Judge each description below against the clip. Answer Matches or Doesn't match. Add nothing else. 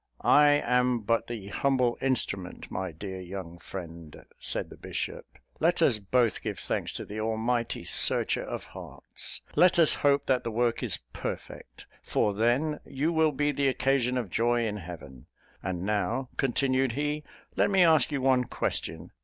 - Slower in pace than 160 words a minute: Doesn't match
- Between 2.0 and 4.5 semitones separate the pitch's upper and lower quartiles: Doesn't match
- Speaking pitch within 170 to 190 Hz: Doesn't match